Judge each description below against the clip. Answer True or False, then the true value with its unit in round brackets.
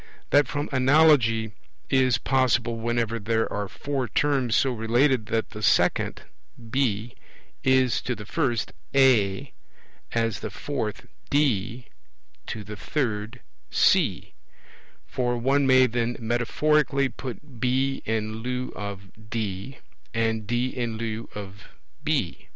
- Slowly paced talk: True (120 wpm)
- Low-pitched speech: True (120 Hz)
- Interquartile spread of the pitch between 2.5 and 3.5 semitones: True (3.0 semitones)